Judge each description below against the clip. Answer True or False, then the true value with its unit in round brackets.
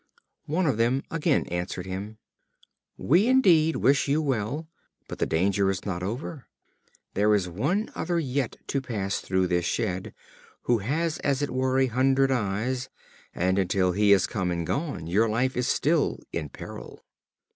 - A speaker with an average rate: True (165 wpm)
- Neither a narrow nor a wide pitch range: False (6.6 semitones)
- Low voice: True (120 Hz)